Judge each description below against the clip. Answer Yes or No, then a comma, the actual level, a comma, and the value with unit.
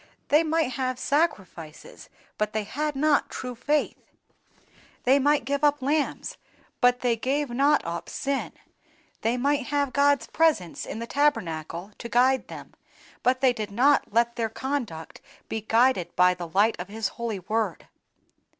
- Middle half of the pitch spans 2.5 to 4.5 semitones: No, average, 5.0 semitones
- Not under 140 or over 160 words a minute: Yes, average, 155 wpm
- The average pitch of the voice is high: Yes, high, 245 Hz